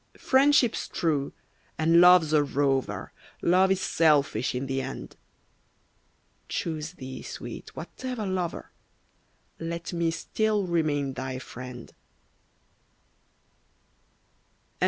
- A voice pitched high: No, medium, 160 Hz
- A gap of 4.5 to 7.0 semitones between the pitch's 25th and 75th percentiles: Yes, average, 4.8 semitones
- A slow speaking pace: Yes, slow, 95 wpm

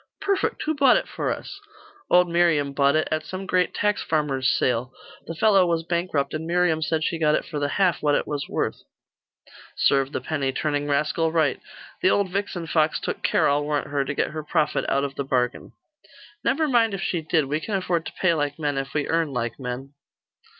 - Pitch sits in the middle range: Yes, medium, 155 Hz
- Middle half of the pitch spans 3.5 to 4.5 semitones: Yes, average, 3.8 semitones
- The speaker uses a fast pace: Yes, fast, 215 wpm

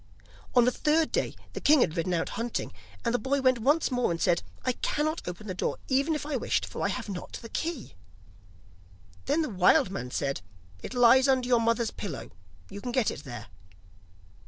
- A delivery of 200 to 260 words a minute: Yes, fast, 205 wpm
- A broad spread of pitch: Yes, wide, 6.0 semitones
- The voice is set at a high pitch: Yes, high, 245 Hz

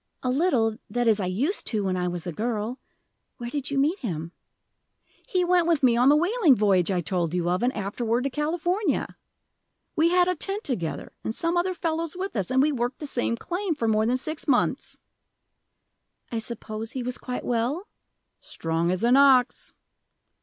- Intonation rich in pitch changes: Yes, wide, 6.8 semitones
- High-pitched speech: Yes, very high, 250 Hz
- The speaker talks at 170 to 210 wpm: Yes, average, 190 wpm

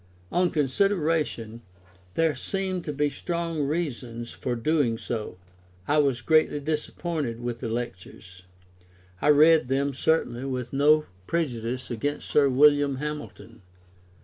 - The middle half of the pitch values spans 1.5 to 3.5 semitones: No, average, 4.4 semitones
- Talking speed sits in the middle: No, slow, 120 wpm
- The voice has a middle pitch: Yes, medium, 145 Hz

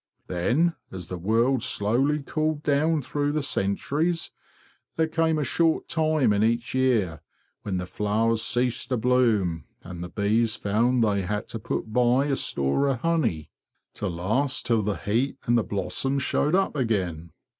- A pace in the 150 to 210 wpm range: Yes, average, 165 wpm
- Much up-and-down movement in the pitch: Yes, wide, 5.8 semitones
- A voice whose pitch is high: No, low, 120 Hz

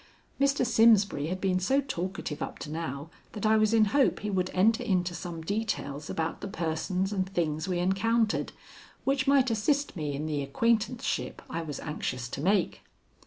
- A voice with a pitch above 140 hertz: Yes, high, 190 Hz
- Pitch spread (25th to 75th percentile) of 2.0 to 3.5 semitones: No, wide, 5.6 semitones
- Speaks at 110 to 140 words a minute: No, average, 175 wpm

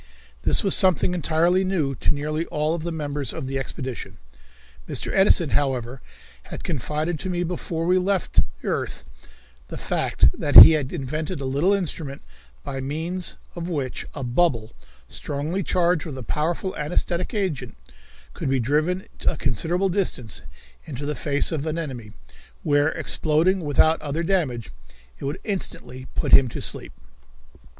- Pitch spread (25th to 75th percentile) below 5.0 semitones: Yes, average, 4.3 semitones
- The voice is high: No, medium, 155 Hz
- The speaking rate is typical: Yes, average, 155 wpm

